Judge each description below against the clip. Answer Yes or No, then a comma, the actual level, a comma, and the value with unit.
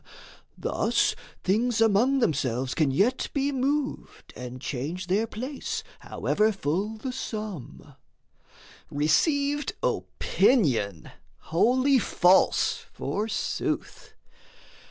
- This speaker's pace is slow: Yes, slow, 85 wpm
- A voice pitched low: No, high, 210 Hz